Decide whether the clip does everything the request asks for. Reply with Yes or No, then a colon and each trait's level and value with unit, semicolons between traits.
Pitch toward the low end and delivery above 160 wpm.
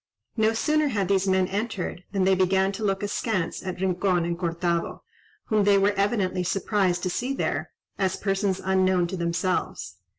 No: high, 190 Hz; average, 170 wpm